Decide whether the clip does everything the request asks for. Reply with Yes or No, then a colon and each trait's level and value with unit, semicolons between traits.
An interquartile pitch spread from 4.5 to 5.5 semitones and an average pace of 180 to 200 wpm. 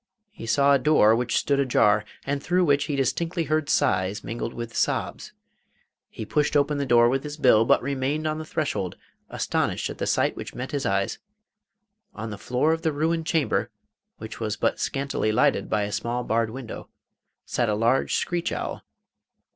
Yes: average, 4.8 semitones; average, 185 wpm